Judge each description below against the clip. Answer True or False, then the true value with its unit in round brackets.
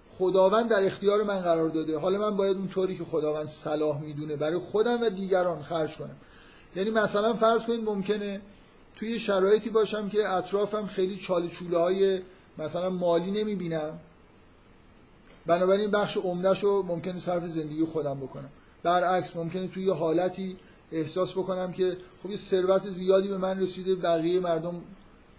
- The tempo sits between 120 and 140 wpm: False (150 wpm)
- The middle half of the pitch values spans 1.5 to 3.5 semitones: True (2.9 semitones)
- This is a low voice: False (185 Hz)